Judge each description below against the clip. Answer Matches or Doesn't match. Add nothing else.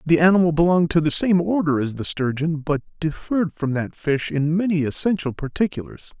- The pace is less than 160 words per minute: Doesn't match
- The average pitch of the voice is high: Doesn't match